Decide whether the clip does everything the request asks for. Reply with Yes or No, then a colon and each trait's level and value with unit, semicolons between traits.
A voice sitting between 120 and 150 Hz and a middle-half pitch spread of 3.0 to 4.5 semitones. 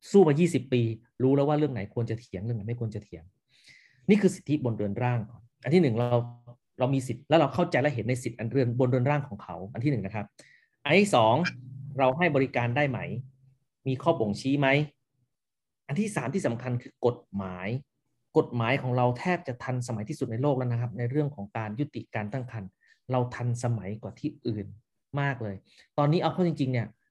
Yes: low, 125 Hz; average, 3.7 semitones